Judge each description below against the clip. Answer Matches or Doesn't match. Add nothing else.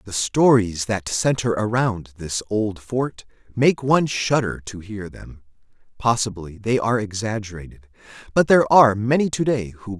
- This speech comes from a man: Matches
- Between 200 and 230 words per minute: Doesn't match